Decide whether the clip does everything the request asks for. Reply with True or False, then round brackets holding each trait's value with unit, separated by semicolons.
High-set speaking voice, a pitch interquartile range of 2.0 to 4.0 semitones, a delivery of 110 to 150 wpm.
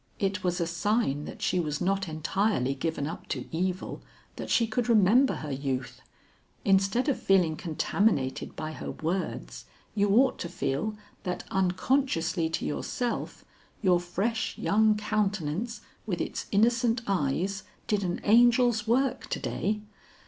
False (195 Hz; 5.0 semitones; 140 wpm)